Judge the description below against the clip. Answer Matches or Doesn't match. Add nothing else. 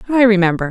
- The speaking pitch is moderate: Doesn't match